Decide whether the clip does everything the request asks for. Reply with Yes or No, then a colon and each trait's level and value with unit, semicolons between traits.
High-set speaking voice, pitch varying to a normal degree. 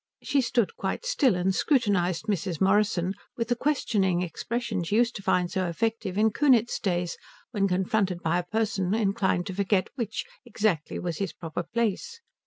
Yes: high, 200 Hz; average, 4.2 semitones